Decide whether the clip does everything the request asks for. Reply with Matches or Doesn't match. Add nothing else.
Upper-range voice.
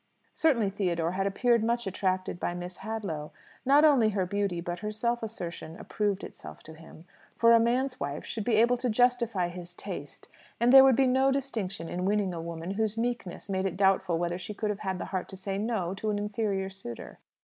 Matches